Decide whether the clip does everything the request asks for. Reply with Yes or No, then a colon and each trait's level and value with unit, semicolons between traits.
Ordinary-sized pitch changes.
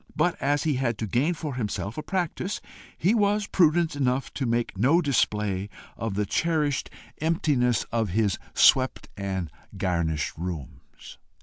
No: wide, 7.6 semitones